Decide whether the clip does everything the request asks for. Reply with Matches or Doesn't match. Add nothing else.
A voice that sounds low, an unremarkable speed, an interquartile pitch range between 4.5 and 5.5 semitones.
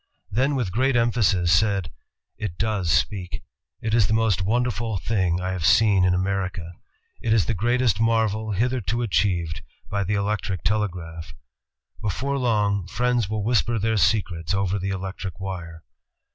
Doesn't match